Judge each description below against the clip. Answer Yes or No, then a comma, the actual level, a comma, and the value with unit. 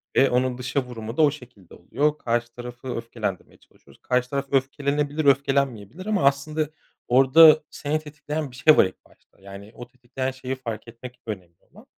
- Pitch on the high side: No, low, 130 Hz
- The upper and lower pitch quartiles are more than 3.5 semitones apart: No, average, 3.2 semitones